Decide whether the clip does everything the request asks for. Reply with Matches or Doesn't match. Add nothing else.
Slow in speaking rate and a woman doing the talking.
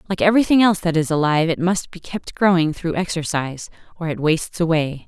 Doesn't match